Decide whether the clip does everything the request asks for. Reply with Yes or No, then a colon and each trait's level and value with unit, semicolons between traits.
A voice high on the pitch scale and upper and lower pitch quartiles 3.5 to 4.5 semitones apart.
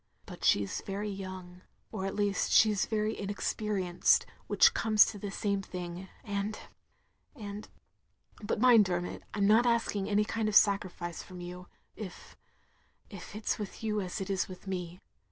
No: high, 200 Hz; narrow, 2.5 semitones